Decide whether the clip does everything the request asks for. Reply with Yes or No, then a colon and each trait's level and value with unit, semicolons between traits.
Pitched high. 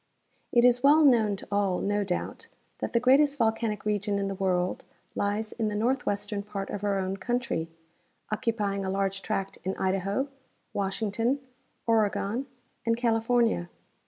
Yes: high, 210 Hz